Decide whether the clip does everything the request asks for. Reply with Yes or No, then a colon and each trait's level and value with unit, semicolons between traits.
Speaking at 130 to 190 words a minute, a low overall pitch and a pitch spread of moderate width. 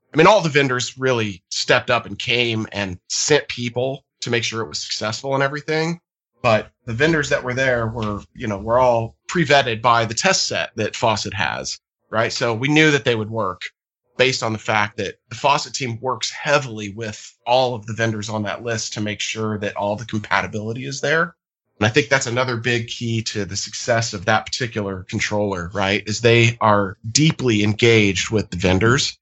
No: average, 200 wpm; low, 115 Hz; average, 3.4 semitones